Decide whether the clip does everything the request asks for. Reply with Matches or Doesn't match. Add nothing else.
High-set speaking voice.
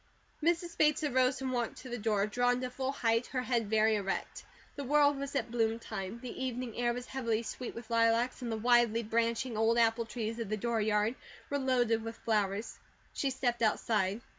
Matches